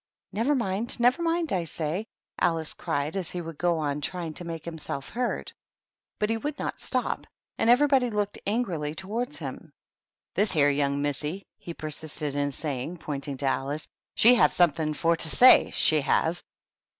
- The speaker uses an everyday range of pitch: No, wide, 6.6 semitones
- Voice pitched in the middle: Yes, medium, 165 Hz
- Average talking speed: Yes, average, 175 wpm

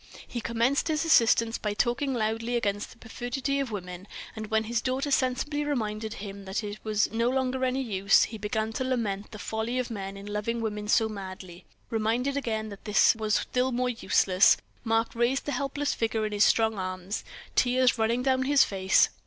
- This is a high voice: Yes, high, 225 Hz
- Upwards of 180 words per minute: Yes, average, 190 wpm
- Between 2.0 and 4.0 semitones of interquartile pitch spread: Yes, average, 3.3 semitones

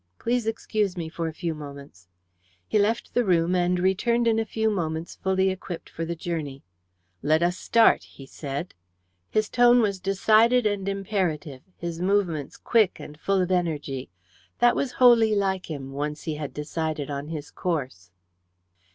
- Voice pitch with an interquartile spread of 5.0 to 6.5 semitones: Yes, wide, 5.5 semitones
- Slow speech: No, average, 165 wpm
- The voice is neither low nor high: Yes, medium, 180 Hz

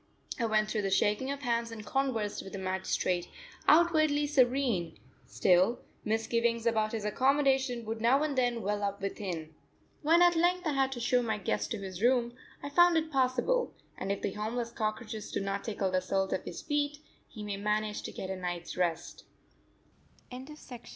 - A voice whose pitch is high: Yes, high, 230 Hz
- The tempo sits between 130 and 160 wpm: No, average, 180 wpm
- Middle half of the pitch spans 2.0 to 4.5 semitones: No, average, 5.2 semitones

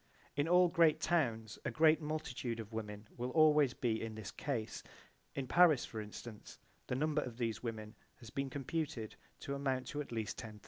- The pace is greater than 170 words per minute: Yes, average, 185 wpm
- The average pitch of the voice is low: Yes, low, 125 Hz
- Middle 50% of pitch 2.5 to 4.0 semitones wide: No, average, 5.3 semitones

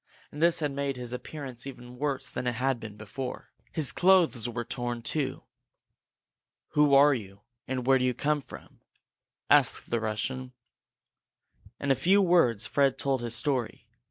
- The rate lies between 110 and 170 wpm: Yes, average, 160 wpm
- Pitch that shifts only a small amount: No, average, 3.0 semitones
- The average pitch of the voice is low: Yes, low, 130 Hz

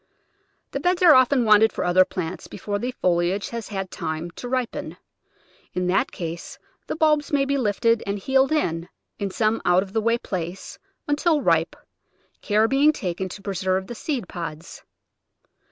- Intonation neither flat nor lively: No, wide, 6.1 semitones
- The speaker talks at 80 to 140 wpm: No, average, 170 wpm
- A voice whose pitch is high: Yes, high, 205 Hz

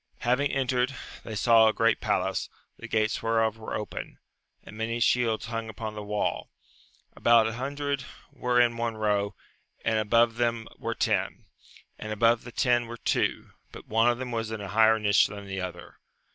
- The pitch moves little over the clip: Yes, narrow, 1.8 semitones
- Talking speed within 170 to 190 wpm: Yes, average, 180 wpm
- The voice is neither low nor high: No, low, 115 Hz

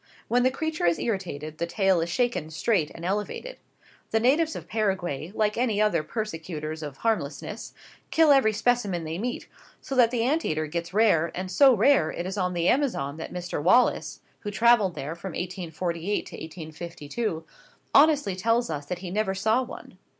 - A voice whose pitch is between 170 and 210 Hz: Yes, high, 190 Hz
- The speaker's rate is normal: Yes, average, 170 wpm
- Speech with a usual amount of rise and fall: No, wide, 5.8 semitones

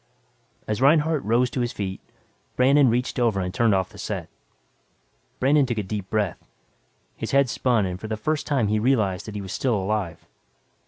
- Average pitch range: Yes, average, 4.4 semitones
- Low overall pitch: Yes, low, 110 Hz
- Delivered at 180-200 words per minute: Yes, average, 190 wpm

